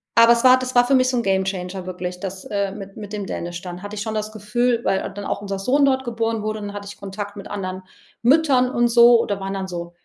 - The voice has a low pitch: No, high, 205 Hz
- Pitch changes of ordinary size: Yes, average, 3.6 semitones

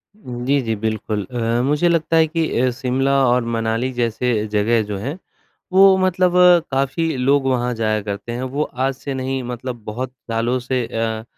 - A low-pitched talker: Yes, low, 125 Hz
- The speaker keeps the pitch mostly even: No, average, 3.3 semitones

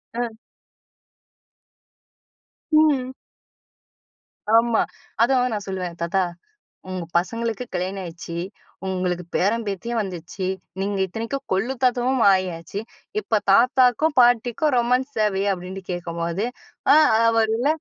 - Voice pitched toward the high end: Yes, high, 215 Hz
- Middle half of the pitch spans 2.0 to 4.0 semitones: No, average, 4.7 semitones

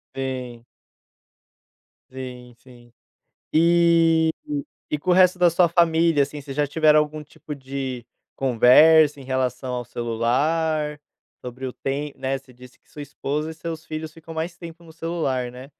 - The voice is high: No, medium, 145 Hz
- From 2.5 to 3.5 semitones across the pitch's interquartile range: No, average, 3.9 semitones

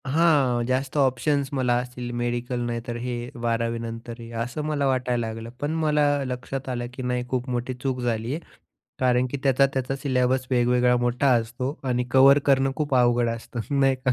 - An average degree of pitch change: No, narrow, 1.9 semitones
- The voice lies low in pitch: Yes, low, 125 Hz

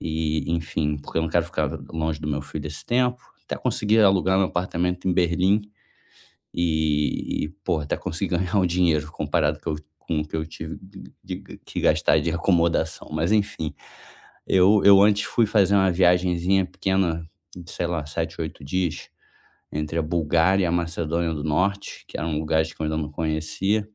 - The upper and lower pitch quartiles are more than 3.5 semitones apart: No, average, 3.2 semitones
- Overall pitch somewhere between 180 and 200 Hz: No, very low, 85 Hz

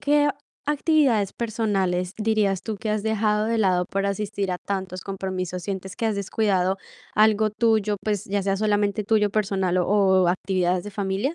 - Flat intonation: Yes, narrow, 2.2 semitones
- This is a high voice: Yes, high, 205 Hz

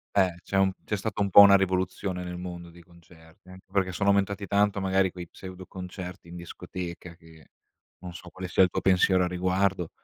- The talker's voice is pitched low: Yes, very low, 90 Hz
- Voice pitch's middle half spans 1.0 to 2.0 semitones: Yes, narrow, 1.6 semitones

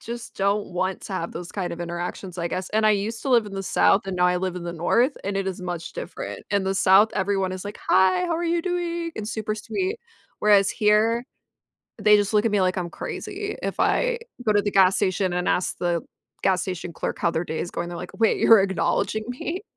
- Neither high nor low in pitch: No, high, 195 Hz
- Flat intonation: No, average, 3.3 semitones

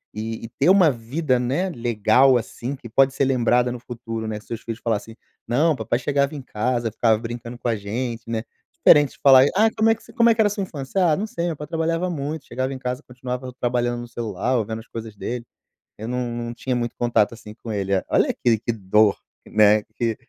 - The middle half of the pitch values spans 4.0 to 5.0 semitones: No, average, 3.3 semitones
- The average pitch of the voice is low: Yes, low, 120 Hz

